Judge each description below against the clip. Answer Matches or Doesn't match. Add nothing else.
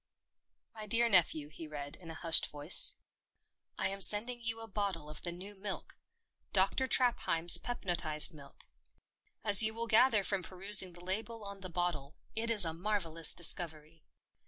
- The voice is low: Doesn't match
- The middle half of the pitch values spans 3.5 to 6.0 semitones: Matches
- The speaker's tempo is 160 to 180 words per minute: Matches